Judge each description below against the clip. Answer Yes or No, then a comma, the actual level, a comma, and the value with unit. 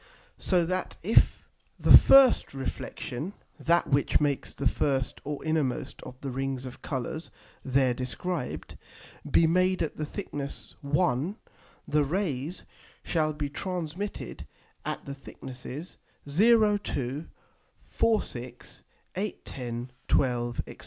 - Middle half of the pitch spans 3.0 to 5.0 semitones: No, wide, 5.6 semitones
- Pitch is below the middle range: No, medium, 145 Hz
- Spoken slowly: Yes, slow, 120 wpm